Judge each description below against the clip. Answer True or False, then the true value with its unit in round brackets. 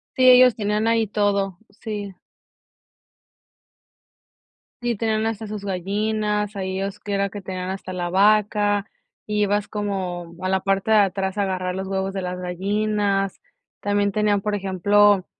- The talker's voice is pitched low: False (200 Hz)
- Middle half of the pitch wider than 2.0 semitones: False (1.7 semitones)